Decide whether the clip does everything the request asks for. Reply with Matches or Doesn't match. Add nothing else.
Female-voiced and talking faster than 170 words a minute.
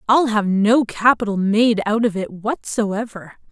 Doesn't match